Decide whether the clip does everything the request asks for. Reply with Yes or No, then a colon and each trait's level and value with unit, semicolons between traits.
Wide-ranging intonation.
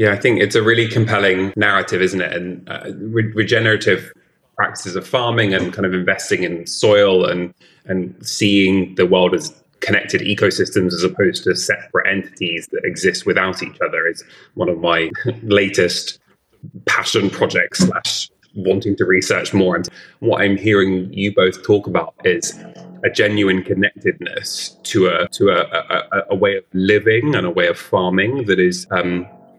No: narrow, 2.4 semitones